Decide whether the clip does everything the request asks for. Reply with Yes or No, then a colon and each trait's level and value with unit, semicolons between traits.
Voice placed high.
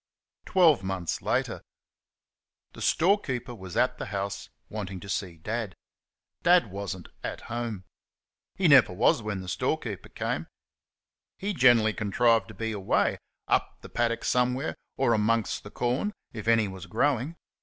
No: low, 115 Hz